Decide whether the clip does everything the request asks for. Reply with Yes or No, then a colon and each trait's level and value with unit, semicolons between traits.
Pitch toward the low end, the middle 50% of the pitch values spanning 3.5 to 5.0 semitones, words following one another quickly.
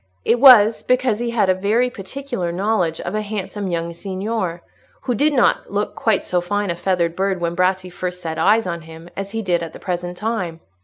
No: high, 190 Hz; average, 4.1 semitones; fast, 210 wpm